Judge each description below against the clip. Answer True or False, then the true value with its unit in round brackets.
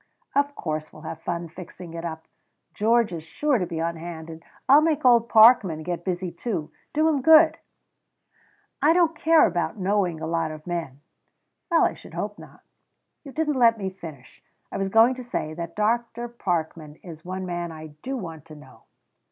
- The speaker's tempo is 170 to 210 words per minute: True (190 wpm)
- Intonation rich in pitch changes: True (6.7 semitones)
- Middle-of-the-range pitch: True (180 Hz)